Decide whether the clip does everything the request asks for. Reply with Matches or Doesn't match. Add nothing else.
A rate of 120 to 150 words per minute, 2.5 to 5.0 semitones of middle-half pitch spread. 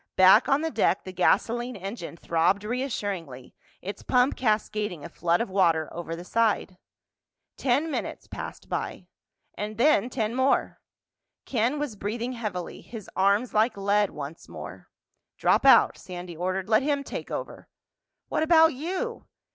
Doesn't match